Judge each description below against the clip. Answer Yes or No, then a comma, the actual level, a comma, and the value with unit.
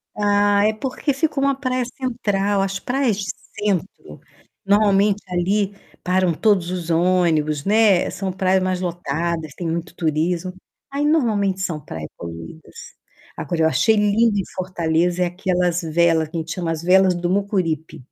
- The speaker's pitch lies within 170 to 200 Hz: Yes, medium, 185 Hz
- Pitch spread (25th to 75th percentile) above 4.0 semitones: No, average, 3.4 semitones